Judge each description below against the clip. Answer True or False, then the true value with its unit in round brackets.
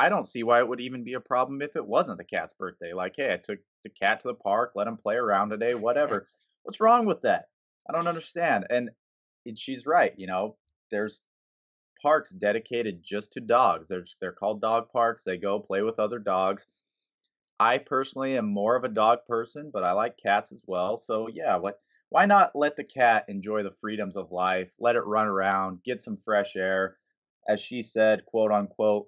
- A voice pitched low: True (110 Hz)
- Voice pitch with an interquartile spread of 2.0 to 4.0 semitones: False (4.4 semitones)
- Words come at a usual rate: False (210 wpm)